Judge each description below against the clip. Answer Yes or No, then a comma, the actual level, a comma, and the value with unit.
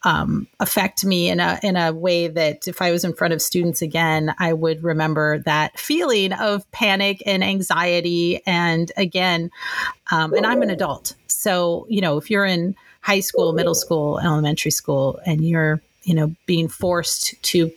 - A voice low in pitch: No, medium, 170 Hz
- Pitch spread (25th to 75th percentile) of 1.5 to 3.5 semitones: Yes, narrow, 2.6 semitones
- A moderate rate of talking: Yes, average, 175 wpm